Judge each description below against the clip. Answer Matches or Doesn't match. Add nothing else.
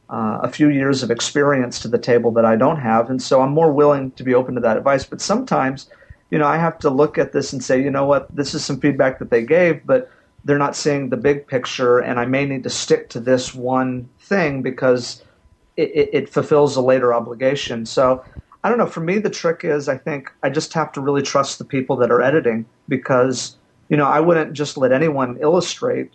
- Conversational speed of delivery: Doesn't match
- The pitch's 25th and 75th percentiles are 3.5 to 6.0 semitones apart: Doesn't match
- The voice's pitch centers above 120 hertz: Matches